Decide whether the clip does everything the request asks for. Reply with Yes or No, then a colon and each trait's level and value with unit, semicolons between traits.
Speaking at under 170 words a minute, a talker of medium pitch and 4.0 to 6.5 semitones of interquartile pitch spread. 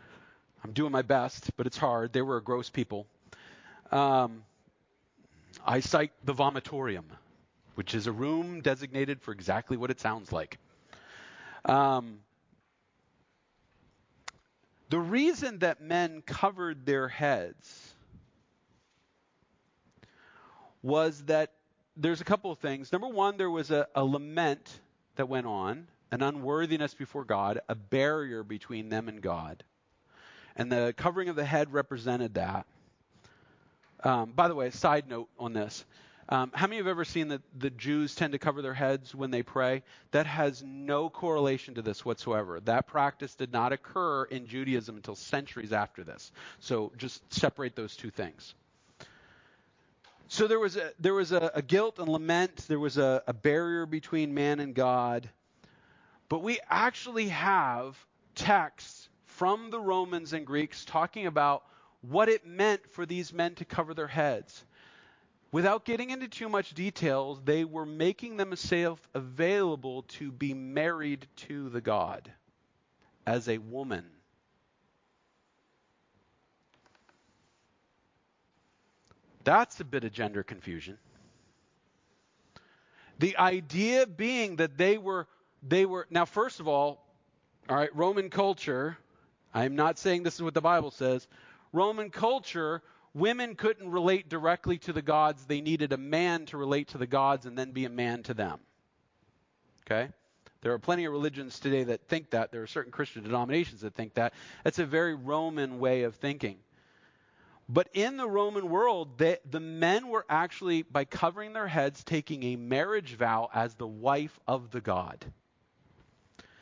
Yes: average, 150 wpm; medium, 145 Hz; average, 5.2 semitones